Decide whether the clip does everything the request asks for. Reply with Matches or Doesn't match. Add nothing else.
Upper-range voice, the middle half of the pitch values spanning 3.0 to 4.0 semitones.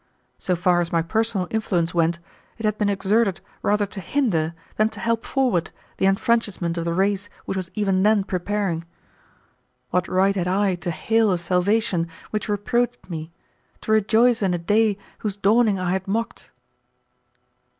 Matches